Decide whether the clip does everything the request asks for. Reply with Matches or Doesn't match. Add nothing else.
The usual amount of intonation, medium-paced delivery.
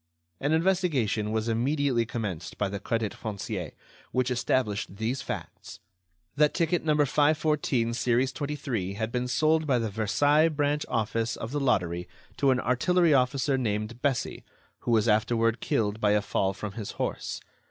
Matches